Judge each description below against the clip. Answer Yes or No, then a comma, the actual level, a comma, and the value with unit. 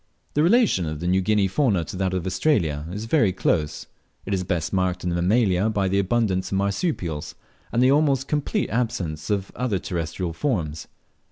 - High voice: No, very low, 95 Hz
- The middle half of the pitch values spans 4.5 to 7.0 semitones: Yes, average, 5.3 semitones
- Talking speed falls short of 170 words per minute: No, average, 190 wpm